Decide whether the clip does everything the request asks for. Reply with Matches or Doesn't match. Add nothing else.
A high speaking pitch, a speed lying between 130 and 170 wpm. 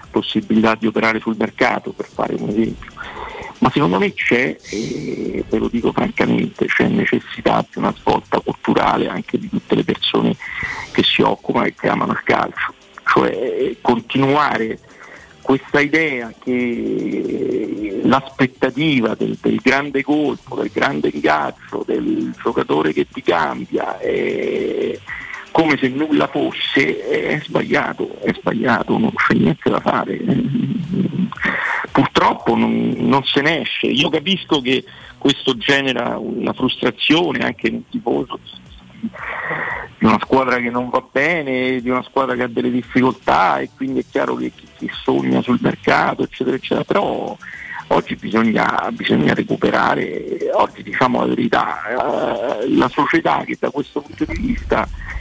Doesn't match